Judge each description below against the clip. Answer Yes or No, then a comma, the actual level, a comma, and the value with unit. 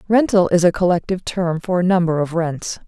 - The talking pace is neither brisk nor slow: No, fast, 210 wpm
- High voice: No, medium, 180 Hz